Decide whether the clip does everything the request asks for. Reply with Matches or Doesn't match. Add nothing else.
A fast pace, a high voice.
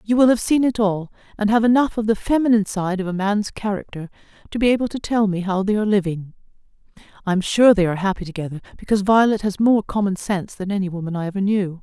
Matches